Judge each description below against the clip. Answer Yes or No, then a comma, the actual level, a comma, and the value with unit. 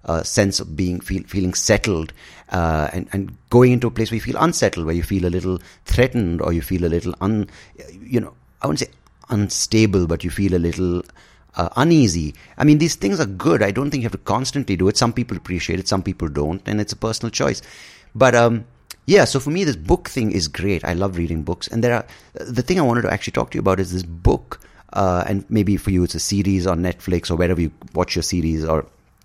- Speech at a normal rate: No, fast, 240 wpm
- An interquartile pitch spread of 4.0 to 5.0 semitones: Yes, average, 4.4 semitones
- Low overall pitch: Yes, very low, 95 Hz